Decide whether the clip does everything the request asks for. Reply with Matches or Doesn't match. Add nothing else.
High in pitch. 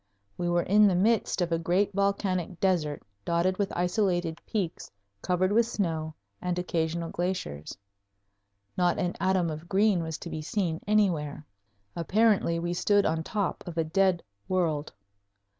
Doesn't match